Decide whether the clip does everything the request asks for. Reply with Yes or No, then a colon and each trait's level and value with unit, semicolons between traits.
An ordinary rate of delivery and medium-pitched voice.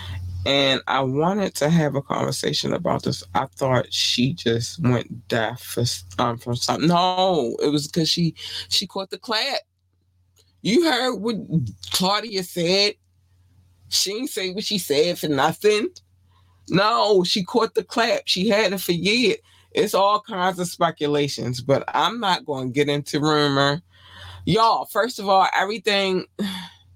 Yes: average, 155 wpm; medium, 155 Hz